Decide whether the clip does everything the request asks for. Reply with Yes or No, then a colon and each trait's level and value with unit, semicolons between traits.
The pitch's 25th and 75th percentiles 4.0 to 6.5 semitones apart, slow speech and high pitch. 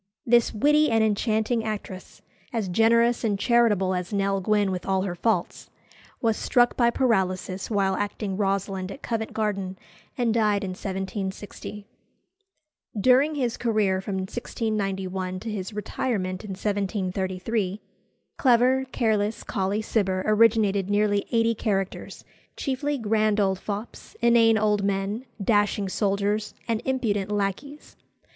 No: average, 2.9 semitones; slow, 125 wpm; high, 210 Hz